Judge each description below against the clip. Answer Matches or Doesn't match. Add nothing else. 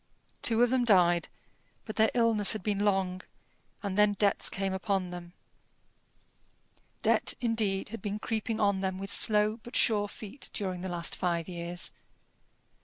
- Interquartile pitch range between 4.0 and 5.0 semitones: Doesn't match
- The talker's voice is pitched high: Matches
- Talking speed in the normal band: Matches